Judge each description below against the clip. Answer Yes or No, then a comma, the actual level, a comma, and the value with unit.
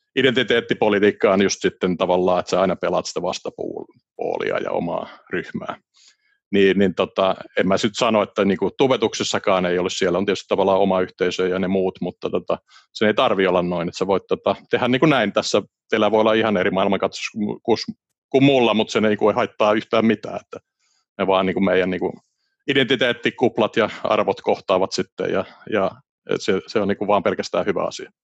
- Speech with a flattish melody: No, average, 3.0 semitones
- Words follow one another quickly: Yes, fast, 185 wpm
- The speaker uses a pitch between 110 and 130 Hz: No, very low, 95 Hz